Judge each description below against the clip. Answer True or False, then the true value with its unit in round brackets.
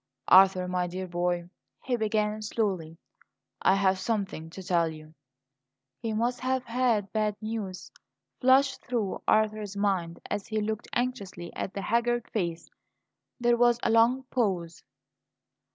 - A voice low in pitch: False (210 Hz)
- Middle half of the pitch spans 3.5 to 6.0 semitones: True (4.2 semitones)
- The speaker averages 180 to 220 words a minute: False (135 wpm)